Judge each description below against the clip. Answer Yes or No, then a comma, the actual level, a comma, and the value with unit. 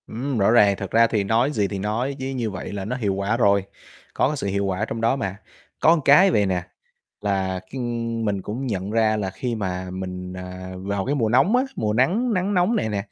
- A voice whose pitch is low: Yes, low, 105 Hz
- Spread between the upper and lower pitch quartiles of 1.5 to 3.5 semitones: No, average, 4.8 semitones